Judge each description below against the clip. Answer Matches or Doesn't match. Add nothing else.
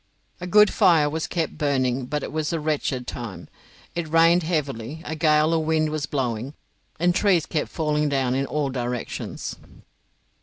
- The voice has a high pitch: Doesn't match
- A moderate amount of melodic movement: Matches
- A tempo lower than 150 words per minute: Doesn't match